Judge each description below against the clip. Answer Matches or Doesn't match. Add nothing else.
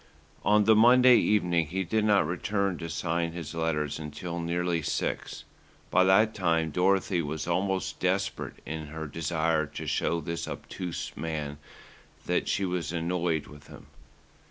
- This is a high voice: Doesn't match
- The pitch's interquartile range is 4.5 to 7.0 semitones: Doesn't match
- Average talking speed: Matches